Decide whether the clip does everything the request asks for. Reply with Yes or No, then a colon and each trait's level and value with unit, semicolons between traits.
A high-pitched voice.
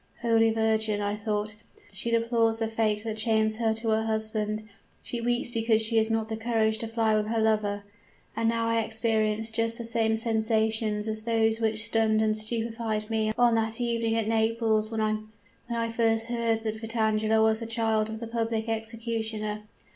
Yes: high, 225 Hz